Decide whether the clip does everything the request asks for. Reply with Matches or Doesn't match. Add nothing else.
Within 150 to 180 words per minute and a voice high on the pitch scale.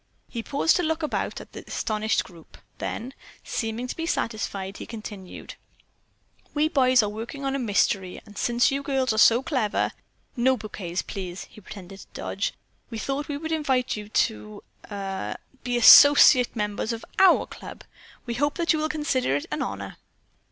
Matches